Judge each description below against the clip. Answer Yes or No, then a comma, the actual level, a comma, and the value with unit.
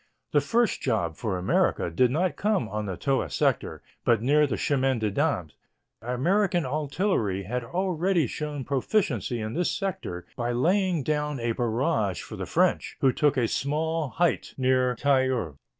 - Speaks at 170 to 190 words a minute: No, average, 160 wpm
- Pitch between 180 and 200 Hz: No, low, 135 Hz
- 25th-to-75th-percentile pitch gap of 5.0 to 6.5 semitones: Yes, wide, 5.6 semitones